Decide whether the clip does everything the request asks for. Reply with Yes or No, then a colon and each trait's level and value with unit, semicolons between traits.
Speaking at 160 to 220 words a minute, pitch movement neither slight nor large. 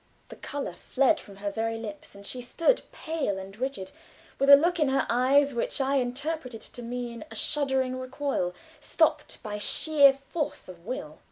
Yes: average, 175 wpm; average, 4.0 semitones